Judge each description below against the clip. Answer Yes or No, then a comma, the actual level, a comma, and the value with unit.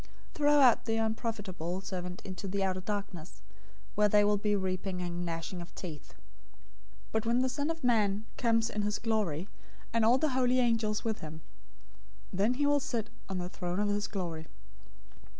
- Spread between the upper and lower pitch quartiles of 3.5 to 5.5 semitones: Yes, average, 3.9 semitones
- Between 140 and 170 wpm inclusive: No, average, 185 wpm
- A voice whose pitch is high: Yes, high, 205 Hz